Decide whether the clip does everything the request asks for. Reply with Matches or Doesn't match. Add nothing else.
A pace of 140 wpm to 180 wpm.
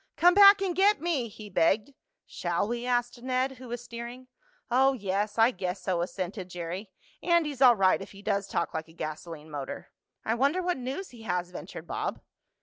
Doesn't match